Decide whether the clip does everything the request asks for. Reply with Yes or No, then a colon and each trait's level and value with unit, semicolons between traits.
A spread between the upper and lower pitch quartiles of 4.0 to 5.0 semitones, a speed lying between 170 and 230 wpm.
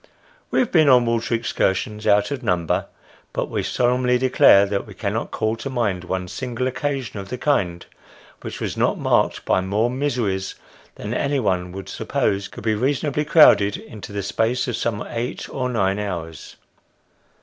Yes: average, 4.5 semitones; average, 175 wpm